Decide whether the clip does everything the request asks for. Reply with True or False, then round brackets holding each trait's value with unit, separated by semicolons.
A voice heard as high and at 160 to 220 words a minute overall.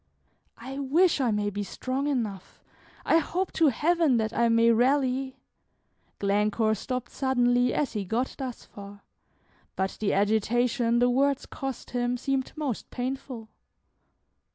False (245 Hz; 140 wpm)